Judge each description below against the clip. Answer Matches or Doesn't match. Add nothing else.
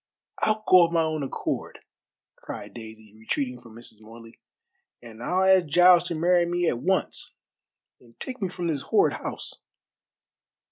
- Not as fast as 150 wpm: Doesn't match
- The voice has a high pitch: Doesn't match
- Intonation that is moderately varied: Doesn't match